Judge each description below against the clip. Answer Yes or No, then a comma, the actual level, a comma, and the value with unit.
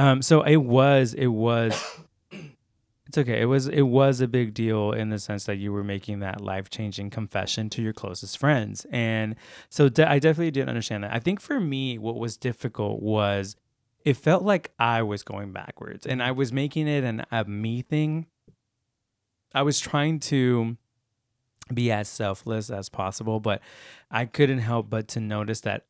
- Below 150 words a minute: No, average, 185 wpm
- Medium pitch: No, low, 115 Hz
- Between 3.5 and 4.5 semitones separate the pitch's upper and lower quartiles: Yes, average, 4.2 semitones